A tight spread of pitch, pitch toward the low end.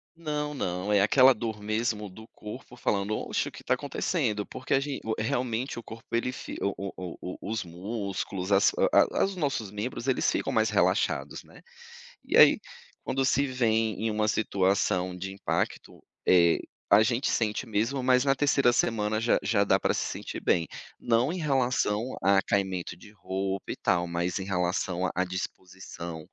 No: average, 4.7 semitones; low, 105 Hz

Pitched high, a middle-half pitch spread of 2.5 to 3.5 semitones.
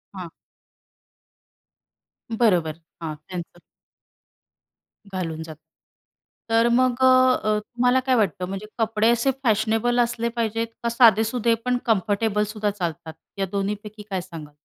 No: high, 215 Hz; average, 3.9 semitones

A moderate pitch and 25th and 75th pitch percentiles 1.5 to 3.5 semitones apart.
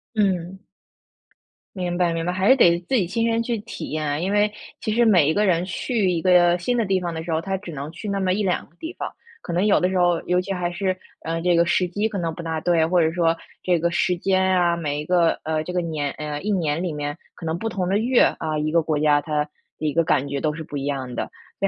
Yes: medium, 175 Hz; average, 3.2 semitones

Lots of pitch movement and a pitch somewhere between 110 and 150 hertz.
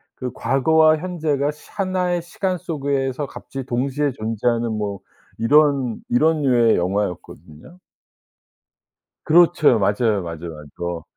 Yes: wide, 6.4 semitones; low, 135 Hz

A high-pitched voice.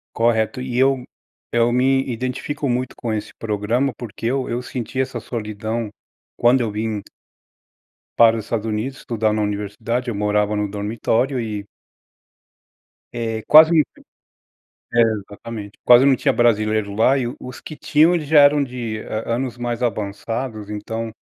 No: low, 115 Hz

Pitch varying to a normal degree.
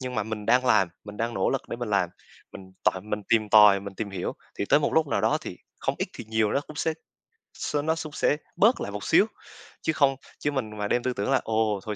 Yes: average, 4.8 semitones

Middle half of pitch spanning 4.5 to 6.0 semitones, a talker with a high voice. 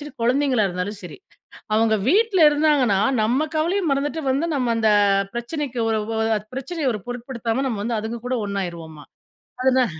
Yes: average, 5.1 semitones; high, 245 Hz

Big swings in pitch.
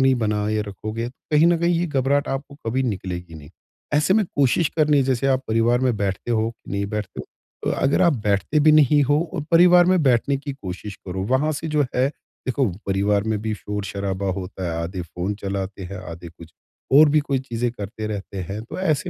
Yes: wide, 6.3 semitones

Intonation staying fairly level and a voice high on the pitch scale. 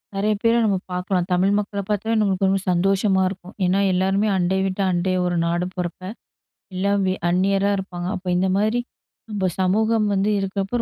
Yes: narrow, 1.7 semitones; high, 195 Hz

